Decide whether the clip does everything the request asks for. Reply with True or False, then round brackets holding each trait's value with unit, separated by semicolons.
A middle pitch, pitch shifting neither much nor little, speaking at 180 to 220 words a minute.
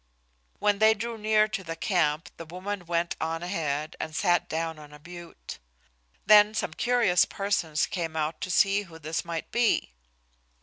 False (175 Hz; 4.2 semitones; 170 wpm)